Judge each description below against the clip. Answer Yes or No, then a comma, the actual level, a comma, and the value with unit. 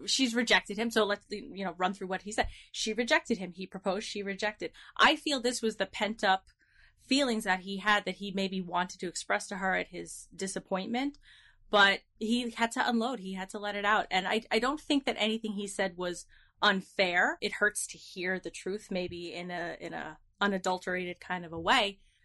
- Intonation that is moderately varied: Yes, average, 3.0 semitones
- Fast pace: Yes, fast, 215 wpm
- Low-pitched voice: No, high, 195 Hz